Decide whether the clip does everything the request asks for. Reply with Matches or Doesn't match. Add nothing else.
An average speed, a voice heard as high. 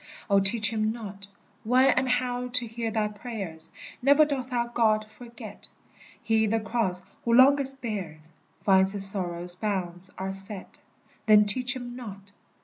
Matches